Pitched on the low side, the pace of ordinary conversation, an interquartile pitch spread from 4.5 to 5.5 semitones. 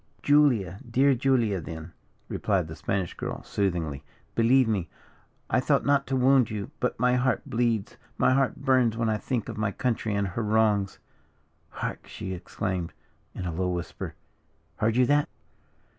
Yes: low, 110 Hz; average, 160 wpm; average, 4.9 semitones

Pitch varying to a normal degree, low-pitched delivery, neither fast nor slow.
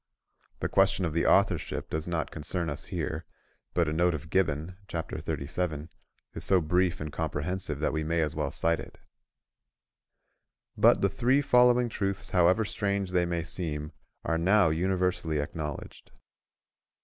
Yes: average, 3.3 semitones; very low, 85 Hz; average, 150 wpm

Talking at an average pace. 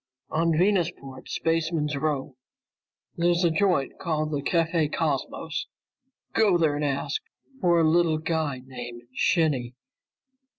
No: slow, 120 wpm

